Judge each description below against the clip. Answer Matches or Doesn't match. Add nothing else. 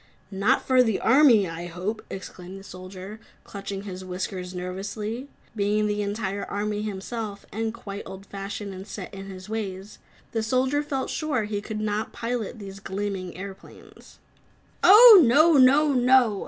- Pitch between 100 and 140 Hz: Doesn't match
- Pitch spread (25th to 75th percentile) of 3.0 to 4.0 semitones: Matches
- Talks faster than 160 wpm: Doesn't match